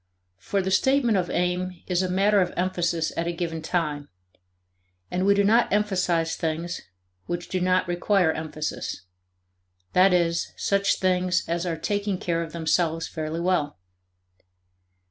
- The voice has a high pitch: No, medium, 180 Hz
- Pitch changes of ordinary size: No, narrow, 2.1 semitones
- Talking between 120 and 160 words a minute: Yes, average, 145 wpm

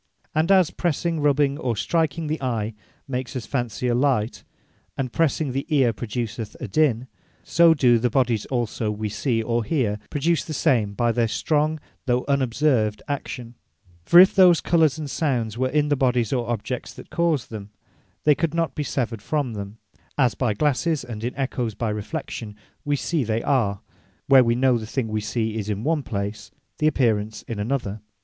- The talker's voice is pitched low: Yes, low, 125 Hz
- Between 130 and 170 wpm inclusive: No, average, 185 wpm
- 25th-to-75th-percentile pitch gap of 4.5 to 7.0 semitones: Yes, average, 4.8 semitones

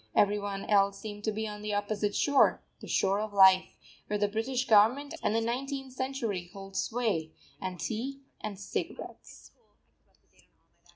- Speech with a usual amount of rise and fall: Yes, average, 3.1 semitones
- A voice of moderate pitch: No, high, 210 Hz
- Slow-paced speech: No, average, 155 wpm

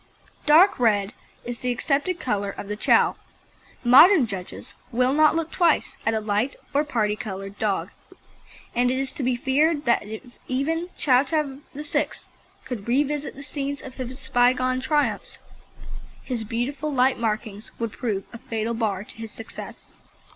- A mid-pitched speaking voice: No, very high, 250 Hz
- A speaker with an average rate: Yes, average, 160 wpm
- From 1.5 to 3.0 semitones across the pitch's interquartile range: No, average, 4.3 semitones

